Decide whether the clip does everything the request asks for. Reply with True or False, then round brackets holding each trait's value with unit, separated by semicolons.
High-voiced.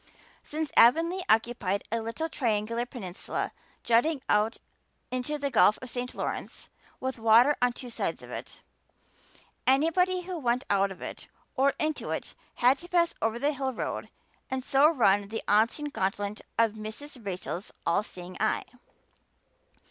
True (245 Hz)